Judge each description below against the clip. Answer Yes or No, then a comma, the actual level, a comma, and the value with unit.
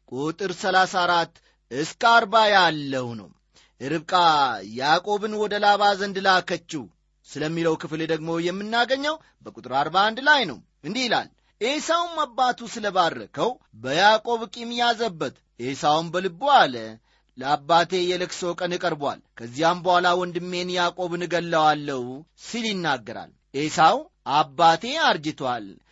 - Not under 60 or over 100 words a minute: No, fast, 110 wpm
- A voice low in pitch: No, medium, 180 Hz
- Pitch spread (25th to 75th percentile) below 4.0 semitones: No, wide, 5.6 semitones